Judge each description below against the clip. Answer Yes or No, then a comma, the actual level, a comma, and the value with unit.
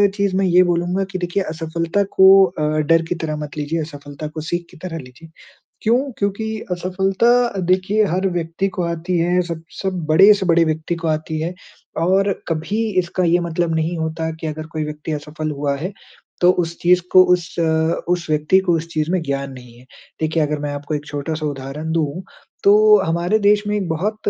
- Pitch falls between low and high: Yes, medium, 165 Hz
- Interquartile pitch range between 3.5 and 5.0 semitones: No, average, 3.0 semitones